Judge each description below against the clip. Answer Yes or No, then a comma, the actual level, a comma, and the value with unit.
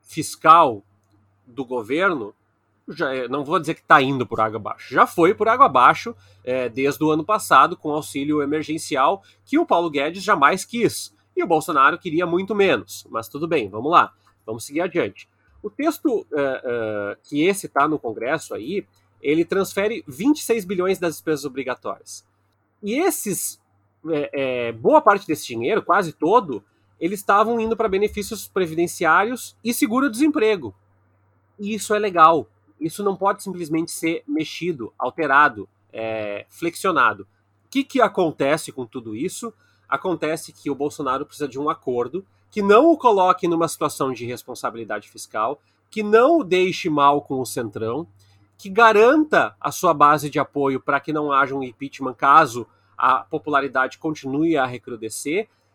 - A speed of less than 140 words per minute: No, average, 155 wpm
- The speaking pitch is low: No, medium, 150 Hz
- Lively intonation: Yes, wide, 8.0 semitones